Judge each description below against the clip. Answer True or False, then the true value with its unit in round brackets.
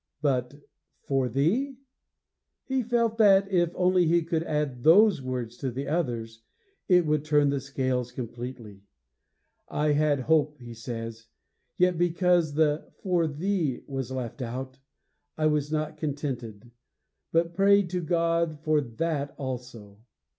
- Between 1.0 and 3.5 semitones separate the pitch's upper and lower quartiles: False (5.1 semitones)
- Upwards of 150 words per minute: False (135 wpm)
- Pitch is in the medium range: True (150 Hz)